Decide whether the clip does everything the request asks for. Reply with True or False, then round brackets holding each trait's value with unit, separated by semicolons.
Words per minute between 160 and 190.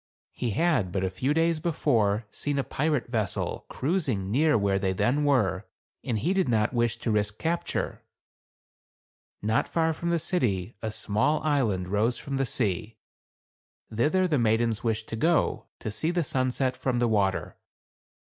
True (165 wpm)